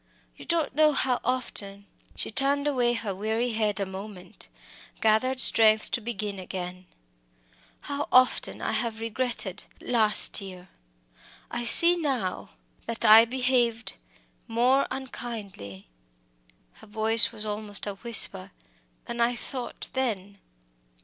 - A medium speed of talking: No, slow, 130 wpm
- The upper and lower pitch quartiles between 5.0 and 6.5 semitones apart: No, average, 3.8 semitones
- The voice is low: No, high, 225 Hz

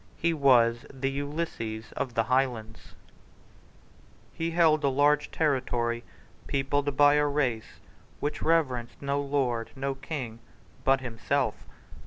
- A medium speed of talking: No, slow, 120 wpm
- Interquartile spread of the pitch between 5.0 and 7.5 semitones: No, average, 3.5 semitones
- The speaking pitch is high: No, low, 135 Hz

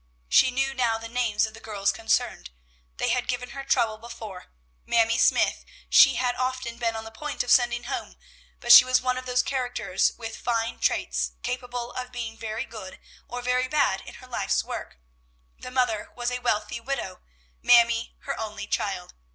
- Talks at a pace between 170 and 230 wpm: Yes, average, 185 wpm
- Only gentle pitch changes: Yes, narrow, 2.1 semitones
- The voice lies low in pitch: No, high, 240 Hz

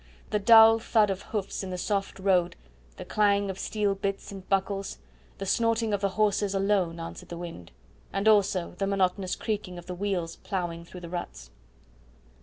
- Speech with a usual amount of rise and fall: No, narrow, 2.2 semitones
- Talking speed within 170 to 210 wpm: Yes, average, 180 wpm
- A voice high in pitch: Yes, high, 195 Hz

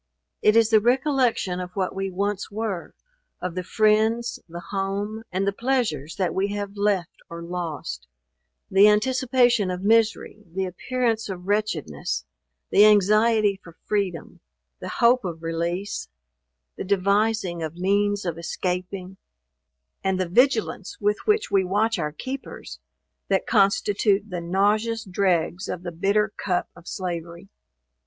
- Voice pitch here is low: No, high, 200 Hz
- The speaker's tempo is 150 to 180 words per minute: No, average, 140 wpm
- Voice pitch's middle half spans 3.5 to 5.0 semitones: No, average, 3.1 semitones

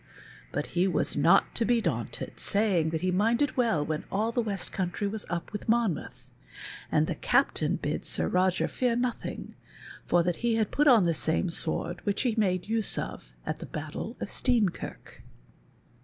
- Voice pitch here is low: No, high, 200 Hz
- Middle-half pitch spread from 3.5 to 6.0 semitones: Yes, average, 4.7 semitones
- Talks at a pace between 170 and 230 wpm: Yes, average, 180 wpm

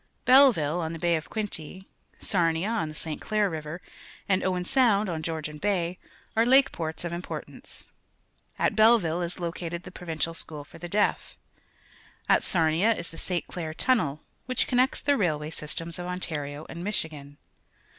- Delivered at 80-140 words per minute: No, average, 175 wpm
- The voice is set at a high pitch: No, medium, 175 Hz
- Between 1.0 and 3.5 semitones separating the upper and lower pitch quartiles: No, average, 4.3 semitones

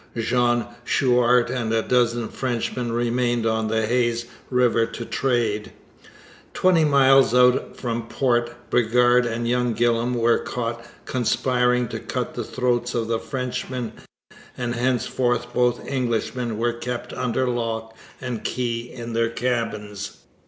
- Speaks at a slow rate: Yes, slow, 130 wpm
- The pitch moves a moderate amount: No, narrow, 1.2 semitones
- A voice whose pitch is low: Yes, low, 120 Hz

